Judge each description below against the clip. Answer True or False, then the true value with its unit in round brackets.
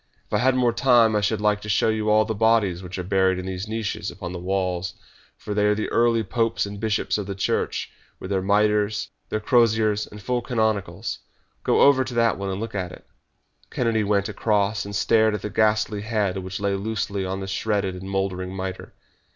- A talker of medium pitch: False (105 Hz)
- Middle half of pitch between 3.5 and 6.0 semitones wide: False (2.4 semitones)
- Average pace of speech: False (215 wpm)